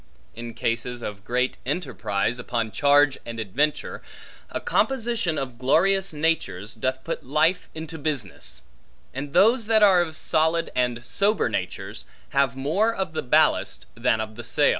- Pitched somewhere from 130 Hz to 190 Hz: Yes, medium, 140 Hz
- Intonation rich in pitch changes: Yes, wide, 5.8 semitones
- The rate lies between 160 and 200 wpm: No, average, 150 wpm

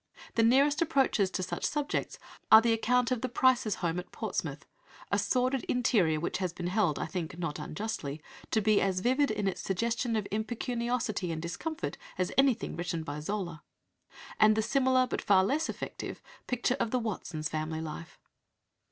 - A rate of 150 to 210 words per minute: Yes, average, 175 wpm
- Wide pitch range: Yes, wide, 6.0 semitones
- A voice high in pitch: Yes, high, 215 Hz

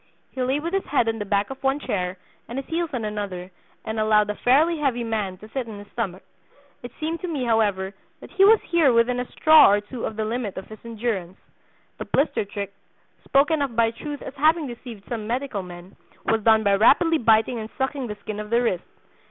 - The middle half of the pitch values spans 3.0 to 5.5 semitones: Yes, average, 4.7 semitones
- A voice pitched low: No, high, 230 Hz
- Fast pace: Yes, fast, 225 wpm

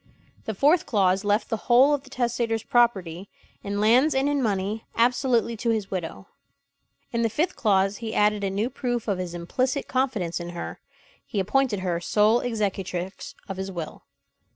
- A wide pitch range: No, average, 4.1 semitones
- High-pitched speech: Yes, high, 215 Hz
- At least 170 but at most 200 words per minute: Yes, average, 175 wpm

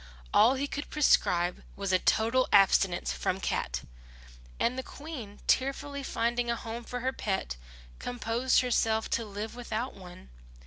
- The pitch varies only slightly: No, average, 4.3 semitones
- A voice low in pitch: No, high, 235 Hz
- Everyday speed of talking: Yes, average, 145 wpm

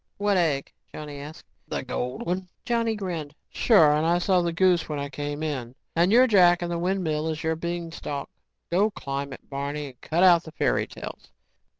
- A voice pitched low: No, medium, 165 Hz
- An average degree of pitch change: Yes, average, 3.7 semitones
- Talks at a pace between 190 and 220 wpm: Yes, average, 195 wpm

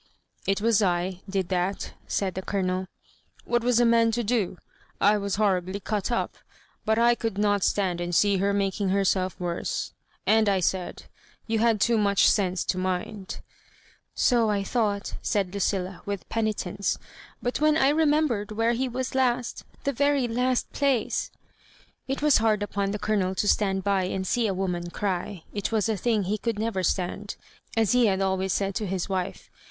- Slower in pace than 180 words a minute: No, average, 190 wpm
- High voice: Yes, high, 205 Hz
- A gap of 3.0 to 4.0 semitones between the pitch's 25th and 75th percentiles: Yes, average, 3.3 semitones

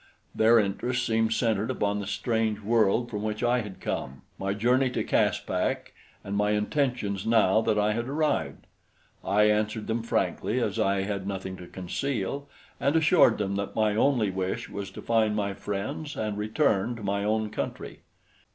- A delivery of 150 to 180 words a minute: Yes, average, 170 wpm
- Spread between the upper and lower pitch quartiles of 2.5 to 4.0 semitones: Yes, average, 2.8 semitones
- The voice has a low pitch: Yes, low, 105 Hz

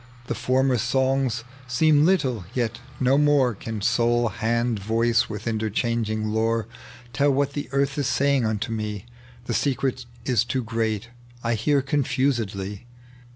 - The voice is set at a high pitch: No, low, 120 Hz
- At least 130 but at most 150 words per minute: Yes, average, 140 wpm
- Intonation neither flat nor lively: Yes, average, 3.5 semitones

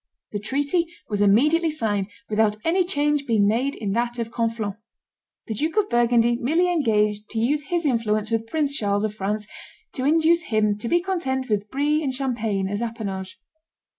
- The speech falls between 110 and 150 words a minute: No, average, 175 wpm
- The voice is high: Yes, high, 235 Hz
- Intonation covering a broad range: Yes, wide, 5.8 semitones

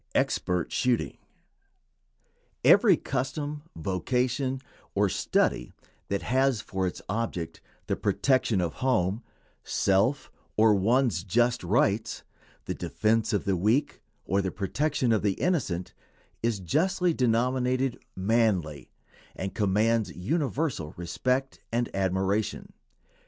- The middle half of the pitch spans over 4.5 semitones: Yes, average, 5.2 semitones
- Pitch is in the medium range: No, low, 110 Hz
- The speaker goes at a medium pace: No, slow, 110 wpm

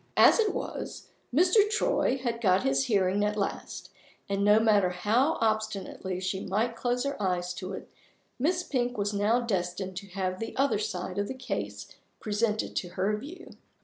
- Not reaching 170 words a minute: No, average, 175 wpm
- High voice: Yes, high, 210 Hz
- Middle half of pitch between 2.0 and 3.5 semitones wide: No, average, 4.6 semitones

